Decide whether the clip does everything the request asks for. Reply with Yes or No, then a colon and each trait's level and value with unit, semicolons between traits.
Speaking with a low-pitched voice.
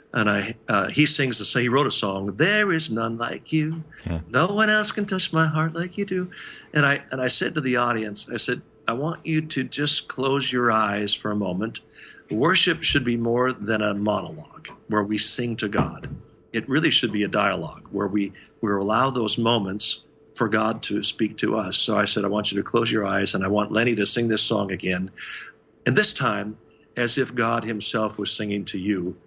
Yes: low, 115 Hz